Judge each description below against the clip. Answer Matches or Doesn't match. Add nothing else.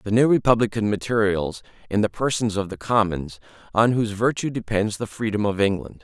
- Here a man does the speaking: Matches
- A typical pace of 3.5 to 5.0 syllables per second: Doesn't match